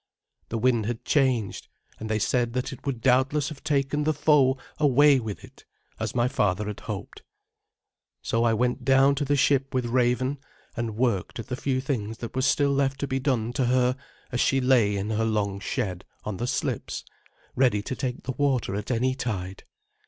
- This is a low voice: Yes, low, 125 Hz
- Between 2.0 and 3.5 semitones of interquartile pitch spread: Yes, average, 3.2 semitones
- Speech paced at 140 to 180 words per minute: No, average, 195 wpm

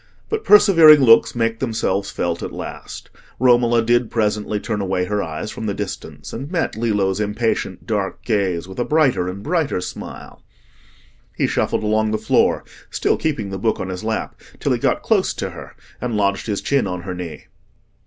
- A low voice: Yes, low, 110 Hz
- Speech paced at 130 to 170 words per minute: No, average, 185 wpm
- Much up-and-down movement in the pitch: No, average, 3.8 semitones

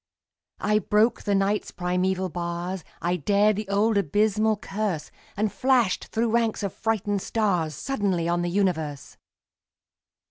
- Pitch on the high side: Yes, high, 200 Hz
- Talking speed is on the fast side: No, slow, 135 wpm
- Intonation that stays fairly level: No, average, 3.2 semitones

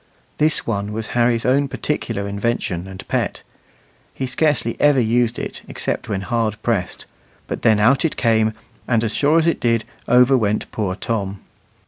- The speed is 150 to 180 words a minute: Yes, average, 165 wpm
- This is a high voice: No, low, 115 Hz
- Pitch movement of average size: Yes, average, 3.2 semitones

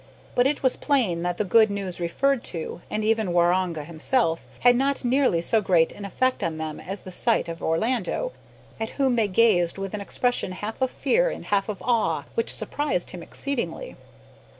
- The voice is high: Yes, high, 210 Hz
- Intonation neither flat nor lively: No, wide, 6.2 semitones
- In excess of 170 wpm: Yes, average, 190 wpm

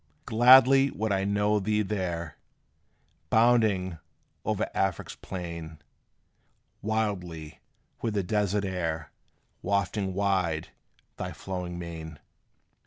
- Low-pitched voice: Yes, very low, 95 Hz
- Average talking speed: No, slow, 95 wpm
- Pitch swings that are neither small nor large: Yes, average, 3.8 semitones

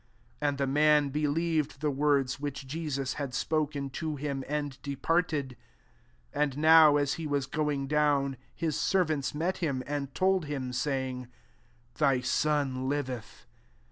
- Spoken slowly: No, average, 160 wpm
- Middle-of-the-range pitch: Yes, medium, 145 Hz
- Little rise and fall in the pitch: Yes, narrow, 2.0 semitones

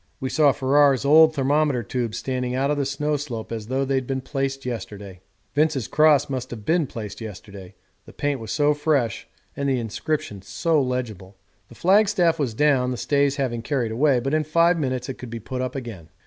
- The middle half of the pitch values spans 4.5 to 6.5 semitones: No, average, 3.8 semitones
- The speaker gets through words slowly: No, average, 200 wpm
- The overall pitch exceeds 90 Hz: Yes, low, 135 Hz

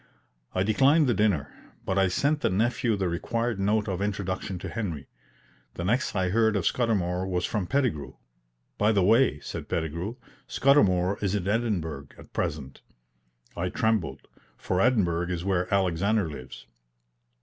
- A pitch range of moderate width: Yes, average, 4.0 semitones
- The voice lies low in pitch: Yes, very low, 95 Hz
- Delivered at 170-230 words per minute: No, average, 150 wpm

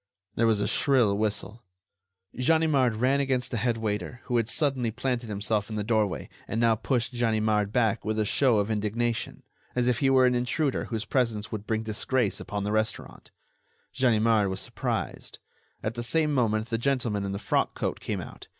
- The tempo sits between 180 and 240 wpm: Yes, average, 185 wpm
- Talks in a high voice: No, low, 115 Hz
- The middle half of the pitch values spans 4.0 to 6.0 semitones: No, average, 2.8 semitones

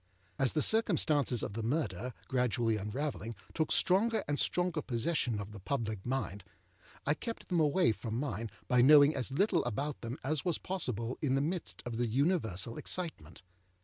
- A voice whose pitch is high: No, low, 135 Hz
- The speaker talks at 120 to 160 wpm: No, average, 170 wpm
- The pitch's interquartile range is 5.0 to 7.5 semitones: Yes, wide, 5.5 semitones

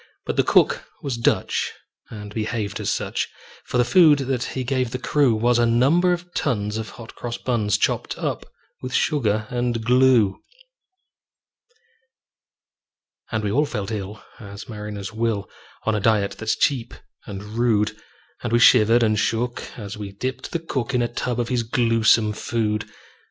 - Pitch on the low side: Yes, low, 115 Hz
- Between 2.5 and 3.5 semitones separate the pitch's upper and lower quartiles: Yes, average, 2.8 semitones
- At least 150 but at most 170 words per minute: Yes, average, 165 wpm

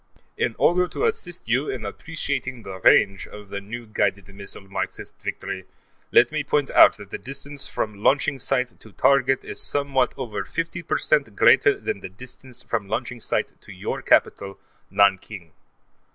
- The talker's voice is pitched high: No, low, 120 Hz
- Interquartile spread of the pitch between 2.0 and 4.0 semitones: No, wide, 5.6 semitones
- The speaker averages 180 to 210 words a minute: No, average, 165 wpm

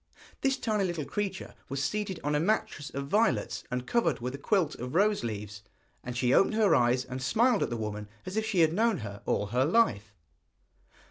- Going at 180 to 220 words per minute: Yes, fast, 205 wpm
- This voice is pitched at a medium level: Yes, medium, 145 Hz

